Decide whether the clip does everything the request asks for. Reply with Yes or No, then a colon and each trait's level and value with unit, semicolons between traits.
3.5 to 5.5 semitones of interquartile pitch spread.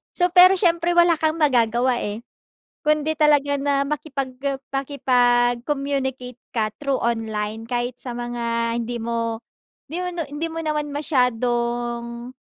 Yes: average, 4.1 semitones